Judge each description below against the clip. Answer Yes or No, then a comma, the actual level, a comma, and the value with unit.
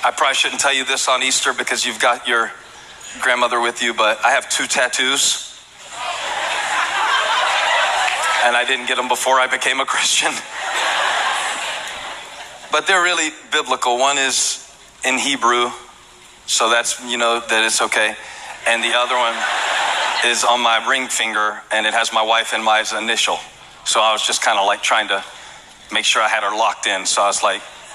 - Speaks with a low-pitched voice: Yes, low, 120 Hz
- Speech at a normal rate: Yes, average, 175 wpm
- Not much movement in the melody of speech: Yes, narrow, 2.3 semitones